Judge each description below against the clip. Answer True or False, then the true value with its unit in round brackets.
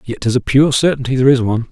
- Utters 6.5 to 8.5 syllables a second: True (7.5 syllables/s)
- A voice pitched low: True (125 Hz)